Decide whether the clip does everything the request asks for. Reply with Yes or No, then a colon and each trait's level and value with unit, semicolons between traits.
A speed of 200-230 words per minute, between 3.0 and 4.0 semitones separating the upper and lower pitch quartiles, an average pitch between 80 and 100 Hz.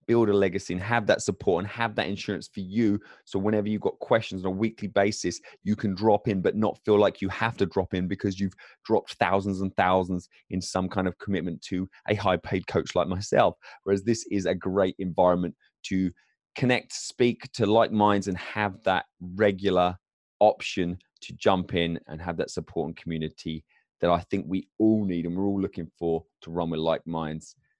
No: fast, 205 wpm; narrow, 2.6 semitones; very low, 95 Hz